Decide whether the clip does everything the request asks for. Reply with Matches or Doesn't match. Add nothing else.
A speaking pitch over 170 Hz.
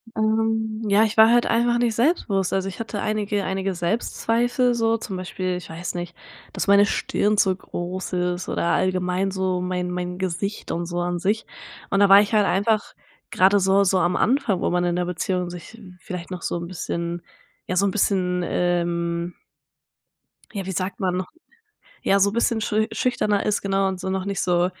Matches